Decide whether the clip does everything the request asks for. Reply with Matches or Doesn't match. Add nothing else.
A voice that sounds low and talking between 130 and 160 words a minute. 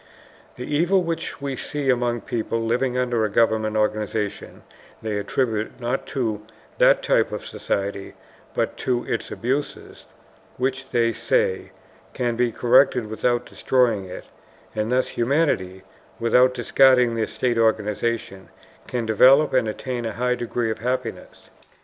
Matches